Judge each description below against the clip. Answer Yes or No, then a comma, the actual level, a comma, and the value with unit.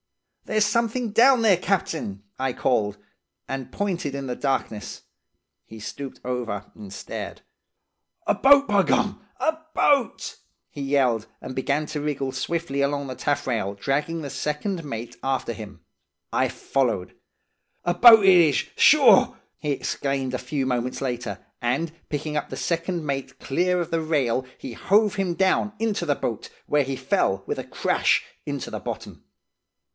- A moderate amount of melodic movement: No, wide, 5.7 semitones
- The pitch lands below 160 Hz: Yes, medium, 140 Hz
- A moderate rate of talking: Yes, average, 160 wpm